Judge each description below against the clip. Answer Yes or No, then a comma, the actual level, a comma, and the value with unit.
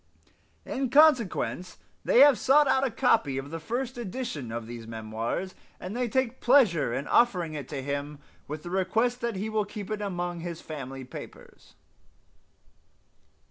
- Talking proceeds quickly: No, average, 160 wpm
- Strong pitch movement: Yes, wide, 9.0 semitones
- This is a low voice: No, medium, 185 Hz